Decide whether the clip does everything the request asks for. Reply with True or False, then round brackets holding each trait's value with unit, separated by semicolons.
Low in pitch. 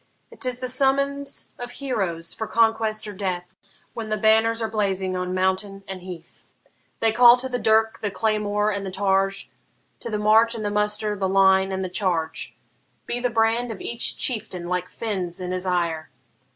False (210 Hz)